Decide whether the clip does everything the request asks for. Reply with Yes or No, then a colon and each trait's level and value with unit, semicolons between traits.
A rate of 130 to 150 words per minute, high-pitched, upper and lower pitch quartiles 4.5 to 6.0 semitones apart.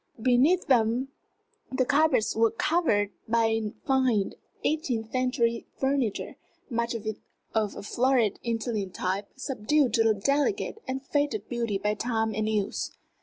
No: slow, 135 wpm; high, 235 Hz; average, 3.5 semitones